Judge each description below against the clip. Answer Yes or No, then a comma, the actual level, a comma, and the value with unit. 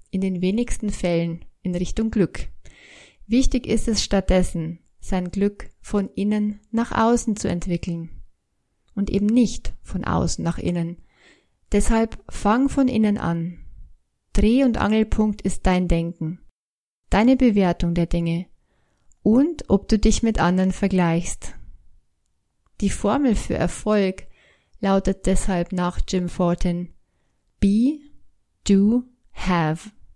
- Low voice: No, high, 195 Hz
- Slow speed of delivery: Yes, slow, 120 wpm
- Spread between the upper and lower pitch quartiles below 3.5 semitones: No, average, 3.9 semitones